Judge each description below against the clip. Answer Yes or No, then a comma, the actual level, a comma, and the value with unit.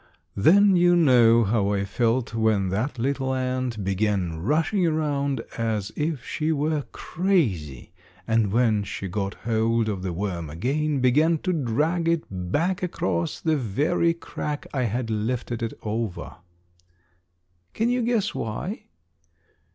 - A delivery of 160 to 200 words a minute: No, slow, 135 wpm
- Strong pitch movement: Yes, wide, 6.8 semitones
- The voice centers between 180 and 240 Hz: No, low, 120 Hz